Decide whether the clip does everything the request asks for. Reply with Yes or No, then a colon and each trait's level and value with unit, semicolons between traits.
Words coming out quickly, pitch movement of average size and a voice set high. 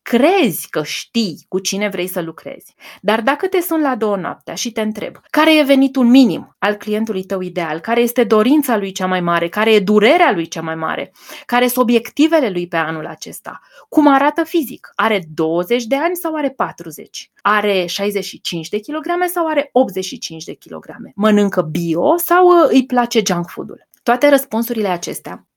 No: fast, 180 wpm; wide, 6.9 semitones; high, 220 Hz